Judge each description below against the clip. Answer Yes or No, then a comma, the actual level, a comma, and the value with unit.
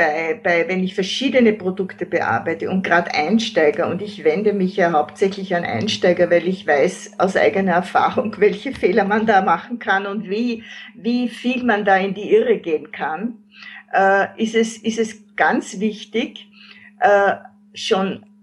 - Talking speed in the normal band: Yes, average, 165 wpm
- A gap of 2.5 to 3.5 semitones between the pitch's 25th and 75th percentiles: Yes, average, 3.2 semitones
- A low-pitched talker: No, high, 205 Hz